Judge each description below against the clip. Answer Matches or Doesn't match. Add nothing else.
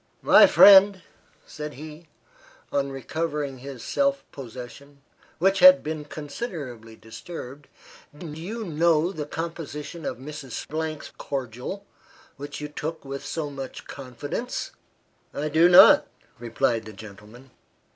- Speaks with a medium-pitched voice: Matches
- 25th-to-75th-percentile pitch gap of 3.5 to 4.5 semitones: Matches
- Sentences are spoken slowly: Matches